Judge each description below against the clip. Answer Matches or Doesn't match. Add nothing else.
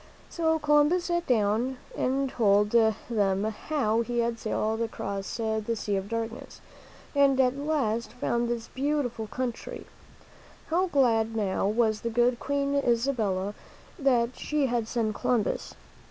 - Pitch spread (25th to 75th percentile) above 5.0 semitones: Doesn't match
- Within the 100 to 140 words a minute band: Matches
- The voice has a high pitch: Matches